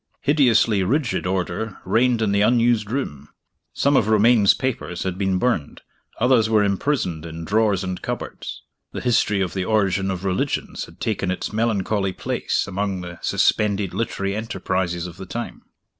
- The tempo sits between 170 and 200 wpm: No, average, 160 wpm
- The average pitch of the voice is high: No, low, 100 Hz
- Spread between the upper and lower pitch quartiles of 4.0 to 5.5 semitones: No, average, 3.5 semitones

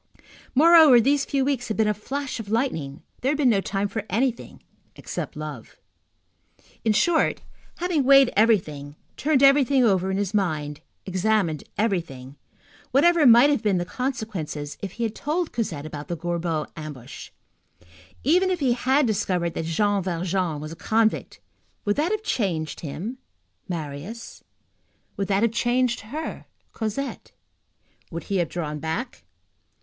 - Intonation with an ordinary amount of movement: No, wide, 7.7 semitones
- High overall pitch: Yes, high, 210 Hz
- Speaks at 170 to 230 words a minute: No, average, 150 wpm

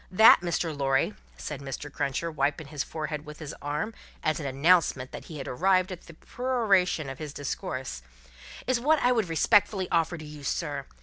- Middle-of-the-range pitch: Yes, medium, 155 Hz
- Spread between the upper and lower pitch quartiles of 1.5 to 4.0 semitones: No, average, 4.5 semitones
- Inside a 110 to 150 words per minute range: No, average, 185 wpm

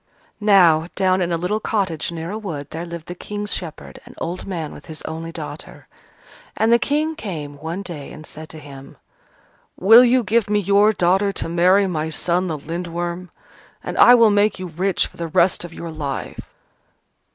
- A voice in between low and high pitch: Yes, medium, 175 Hz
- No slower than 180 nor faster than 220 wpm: Yes, average, 190 wpm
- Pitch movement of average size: Yes, average, 3.9 semitones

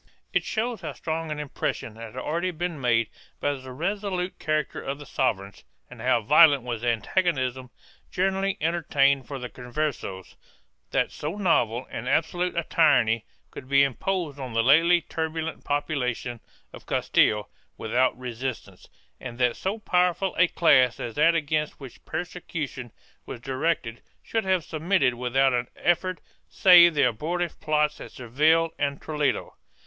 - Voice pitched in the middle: Yes, medium, 145 Hz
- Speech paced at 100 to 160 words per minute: Yes, average, 150 wpm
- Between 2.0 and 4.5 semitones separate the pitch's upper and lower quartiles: No, average, 5.1 semitones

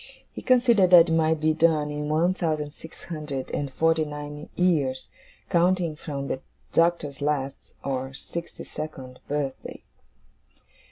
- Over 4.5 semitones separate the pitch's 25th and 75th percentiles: No, average, 2.8 semitones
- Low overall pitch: No, medium, 155 Hz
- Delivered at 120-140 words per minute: Yes, slow, 135 wpm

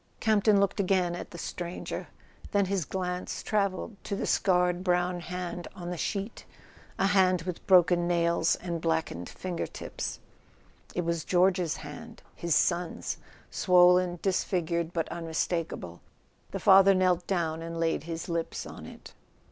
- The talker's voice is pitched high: No, medium, 180 Hz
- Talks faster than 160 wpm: No, average, 145 wpm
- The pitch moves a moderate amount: No, narrow, 1.8 semitones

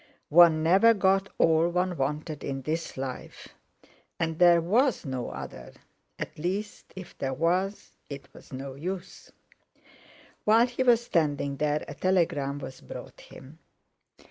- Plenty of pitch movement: No, average, 5.0 semitones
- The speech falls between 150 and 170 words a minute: No, slow, 135 wpm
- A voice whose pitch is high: No, medium, 165 Hz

